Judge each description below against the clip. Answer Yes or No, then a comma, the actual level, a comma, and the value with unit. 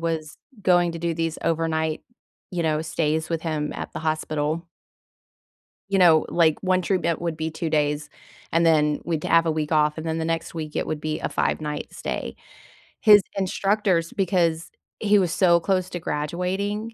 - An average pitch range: No, narrow, 2.2 semitones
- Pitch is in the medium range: Yes, medium, 165 Hz